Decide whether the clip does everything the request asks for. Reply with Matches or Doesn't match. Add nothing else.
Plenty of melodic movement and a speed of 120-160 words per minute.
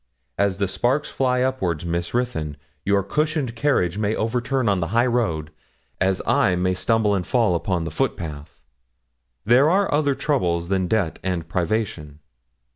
Matches